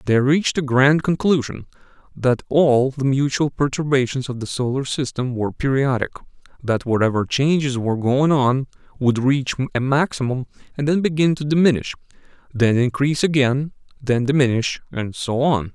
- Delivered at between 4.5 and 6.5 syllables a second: Yes, 5.1 syllables/s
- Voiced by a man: Yes, male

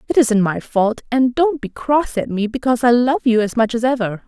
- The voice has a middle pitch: No, high, 240 Hz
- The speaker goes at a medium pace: No, fast, 255 wpm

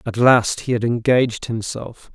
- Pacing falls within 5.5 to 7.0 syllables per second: No, 4.5 syllables/s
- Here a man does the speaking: Yes, male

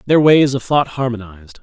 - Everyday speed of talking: Yes, average, 185 wpm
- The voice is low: Yes, low, 125 Hz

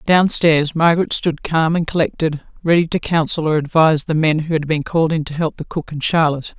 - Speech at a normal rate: No, fast, 230 wpm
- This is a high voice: No, medium, 160 Hz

